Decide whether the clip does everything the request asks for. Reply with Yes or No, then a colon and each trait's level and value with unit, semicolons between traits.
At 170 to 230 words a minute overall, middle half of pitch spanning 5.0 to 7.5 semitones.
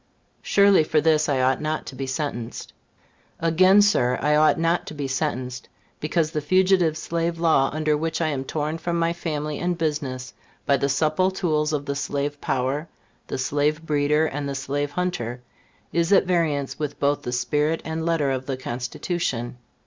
No: average, 180 wpm; average, 3.1 semitones